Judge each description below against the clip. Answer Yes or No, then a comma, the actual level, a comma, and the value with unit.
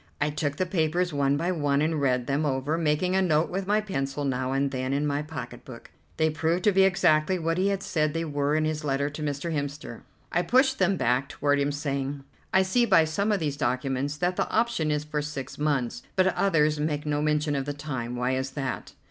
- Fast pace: Yes, fast, 230 wpm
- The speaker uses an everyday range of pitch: Yes, average, 3.3 semitones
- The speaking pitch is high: No, medium, 150 Hz